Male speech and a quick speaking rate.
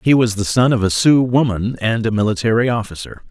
Yes: male; fast, 220 wpm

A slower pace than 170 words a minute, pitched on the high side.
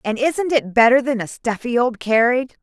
No: fast, 205 wpm; high, 245 Hz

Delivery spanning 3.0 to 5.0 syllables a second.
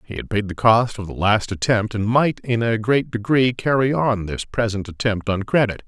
Yes: 4.9 syllables/s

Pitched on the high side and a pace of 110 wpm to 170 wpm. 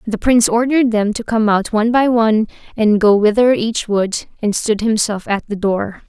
No: high, 220 Hz; fast, 205 wpm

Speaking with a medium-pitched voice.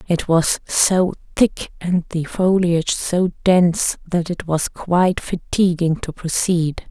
Yes: medium, 175 Hz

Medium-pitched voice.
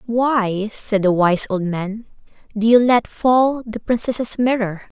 No: high, 220 Hz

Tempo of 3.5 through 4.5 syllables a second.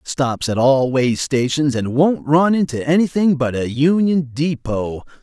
Yes: 4.0 syllables/s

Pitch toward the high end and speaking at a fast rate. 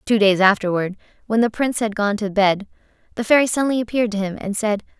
Yes: high, 215 Hz; fast, 215 wpm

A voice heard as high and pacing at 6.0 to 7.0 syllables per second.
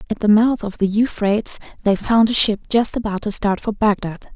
No: high, 210 Hz; 5.4 syllables/s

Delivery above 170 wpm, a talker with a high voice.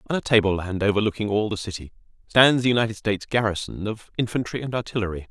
No: average, 190 wpm; low, 105 Hz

